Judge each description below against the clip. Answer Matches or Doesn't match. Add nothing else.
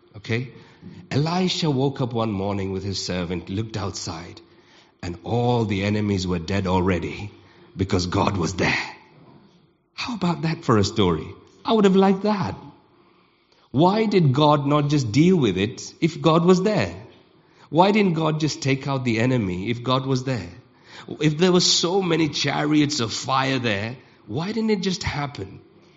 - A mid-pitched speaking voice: Doesn't match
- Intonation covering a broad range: Matches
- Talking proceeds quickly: Doesn't match